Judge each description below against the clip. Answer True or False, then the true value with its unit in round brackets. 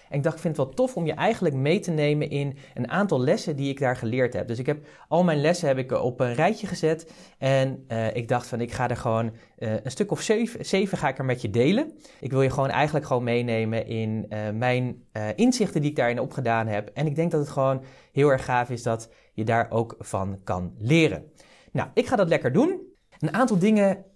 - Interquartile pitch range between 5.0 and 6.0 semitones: True (5.6 semitones)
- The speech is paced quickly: True (245 wpm)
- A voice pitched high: False (135 Hz)